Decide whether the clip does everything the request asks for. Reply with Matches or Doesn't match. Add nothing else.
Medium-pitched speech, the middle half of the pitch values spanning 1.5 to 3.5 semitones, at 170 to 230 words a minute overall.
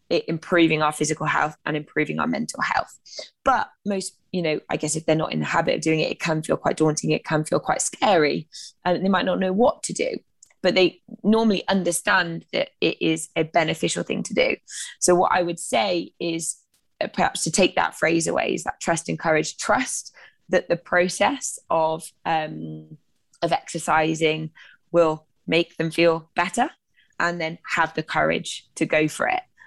Matches